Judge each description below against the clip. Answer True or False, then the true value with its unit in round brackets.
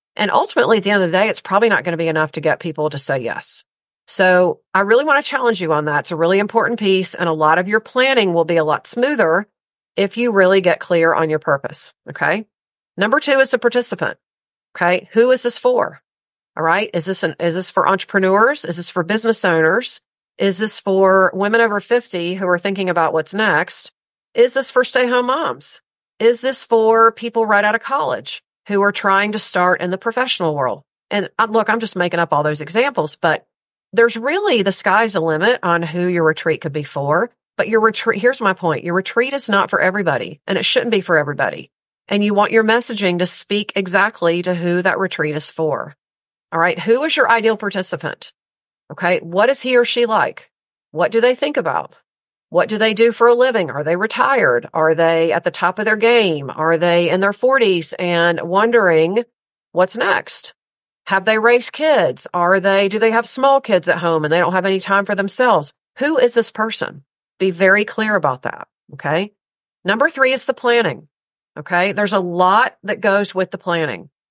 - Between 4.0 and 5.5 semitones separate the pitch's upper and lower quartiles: True (5.1 semitones)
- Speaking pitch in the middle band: False (195 Hz)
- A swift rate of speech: True (210 wpm)